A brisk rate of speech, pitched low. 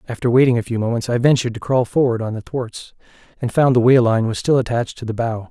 Yes: fast, 260 wpm; low, 120 Hz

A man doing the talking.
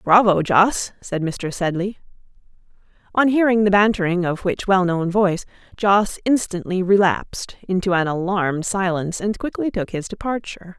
No: female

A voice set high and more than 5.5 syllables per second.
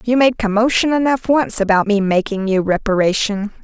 No: high, 220 Hz; 5.2 syllables/s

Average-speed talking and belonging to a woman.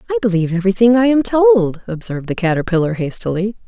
Yes: average, 165 wpm; female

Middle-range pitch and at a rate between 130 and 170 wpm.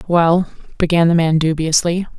Yes: medium, 165 Hz; slow, 135 wpm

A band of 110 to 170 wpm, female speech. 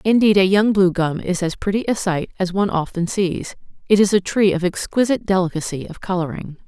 No: fast, 205 wpm; female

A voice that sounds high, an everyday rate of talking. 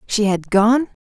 Yes: high, 215 Hz; average, 175 wpm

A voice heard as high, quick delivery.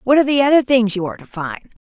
Yes: high, 240 Hz; fast, 295 wpm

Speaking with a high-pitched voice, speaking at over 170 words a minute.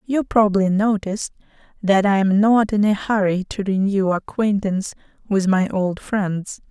No: high, 200 Hz; average, 150 wpm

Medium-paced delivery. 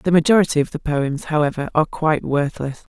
Yes: average, 180 wpm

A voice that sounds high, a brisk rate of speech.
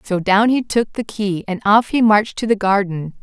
Yes: high, 205 Hz; fast, 240 wpm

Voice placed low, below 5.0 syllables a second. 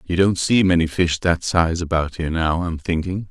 No: very low, 85 Hz; 5.1 syllables/s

